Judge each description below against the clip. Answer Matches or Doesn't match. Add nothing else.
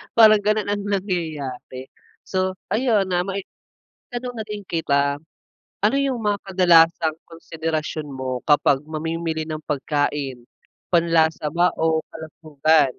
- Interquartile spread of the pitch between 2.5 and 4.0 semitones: Doesn't match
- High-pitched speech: Doesn't match